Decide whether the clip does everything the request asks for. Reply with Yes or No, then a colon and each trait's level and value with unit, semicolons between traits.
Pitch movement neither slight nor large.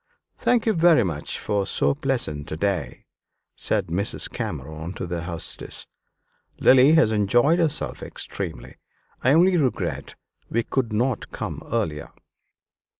No: wide, 8.9 semitones